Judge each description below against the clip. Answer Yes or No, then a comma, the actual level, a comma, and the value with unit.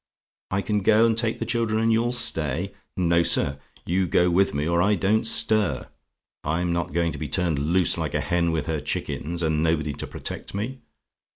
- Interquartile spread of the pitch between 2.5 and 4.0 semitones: No, average, 5.0 semitones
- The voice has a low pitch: Yes, very low, 85 Hz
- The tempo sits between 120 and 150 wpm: No, average, 200 wpm